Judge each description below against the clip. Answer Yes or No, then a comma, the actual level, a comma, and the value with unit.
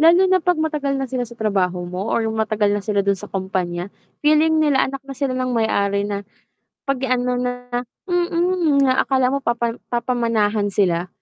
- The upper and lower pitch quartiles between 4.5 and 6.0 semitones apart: Yes, average, 5.1 semitones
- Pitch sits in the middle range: No, high, 245 Hz